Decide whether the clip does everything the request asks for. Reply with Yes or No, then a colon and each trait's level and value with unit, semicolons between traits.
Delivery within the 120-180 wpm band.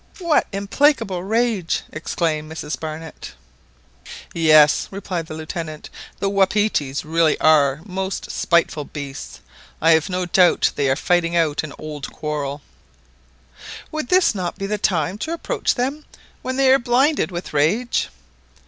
Yes: average, 140 wpm